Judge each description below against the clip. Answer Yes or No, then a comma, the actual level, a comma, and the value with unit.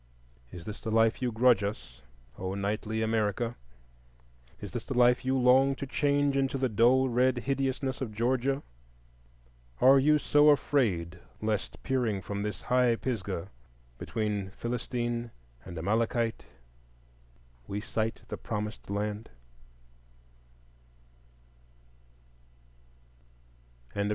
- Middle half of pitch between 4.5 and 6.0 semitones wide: No, average, 3.8 semitones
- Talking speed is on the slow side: Yes, slow, 110 wpm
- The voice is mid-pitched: No, low, 115 Hz